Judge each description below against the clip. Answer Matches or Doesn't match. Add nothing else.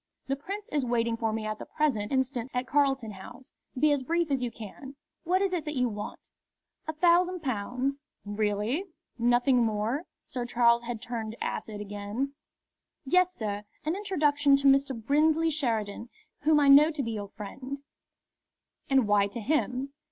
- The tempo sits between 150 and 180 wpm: Matches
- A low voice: Doesn't match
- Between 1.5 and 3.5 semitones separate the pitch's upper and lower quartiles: Doesn't match